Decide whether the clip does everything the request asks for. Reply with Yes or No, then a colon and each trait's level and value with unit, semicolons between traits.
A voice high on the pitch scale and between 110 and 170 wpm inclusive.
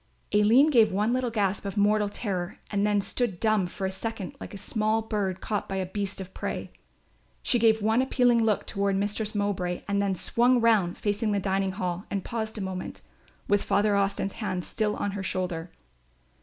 No: high, 205 Hz; average, 195 wpm